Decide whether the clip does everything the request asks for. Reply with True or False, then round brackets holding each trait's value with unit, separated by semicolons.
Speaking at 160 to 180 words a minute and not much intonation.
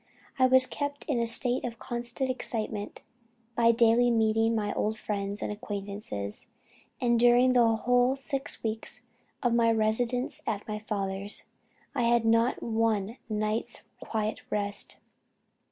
False (135 wpm; 2.3 semitones)